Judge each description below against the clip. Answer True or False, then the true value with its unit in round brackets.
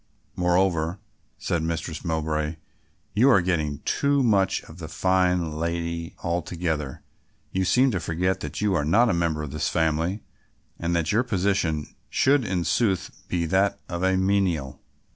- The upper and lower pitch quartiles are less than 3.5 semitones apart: True (2.9 semitones)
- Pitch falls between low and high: False (85 Hz)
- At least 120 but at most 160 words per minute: True (155 wpm)